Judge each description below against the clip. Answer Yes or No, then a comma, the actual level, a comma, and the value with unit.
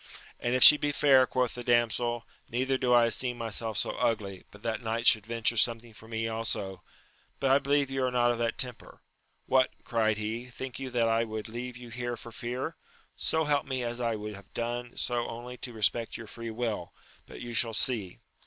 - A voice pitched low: Yes, low, 120 Hz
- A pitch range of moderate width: No, narrow, 1.8 semitones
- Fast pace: Yes, fast, 210 wpm